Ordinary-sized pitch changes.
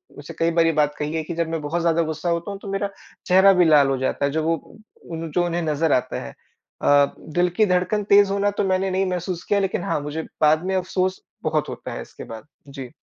Yes: average, 3.5 semitones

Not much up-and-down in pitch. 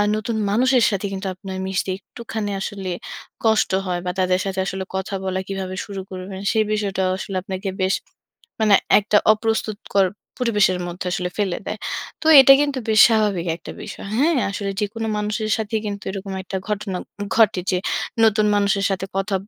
Yes: narrow, 2.3 semitones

